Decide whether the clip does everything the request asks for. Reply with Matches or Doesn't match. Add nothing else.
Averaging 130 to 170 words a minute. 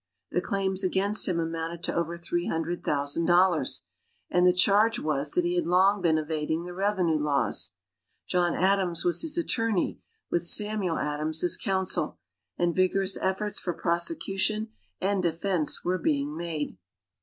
Matches